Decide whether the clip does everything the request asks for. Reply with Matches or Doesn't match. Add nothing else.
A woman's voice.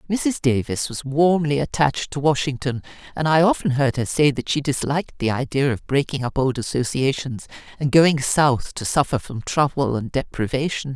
Matches